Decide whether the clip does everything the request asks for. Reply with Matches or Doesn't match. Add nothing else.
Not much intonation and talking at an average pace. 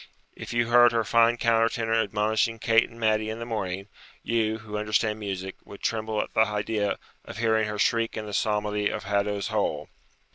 Matches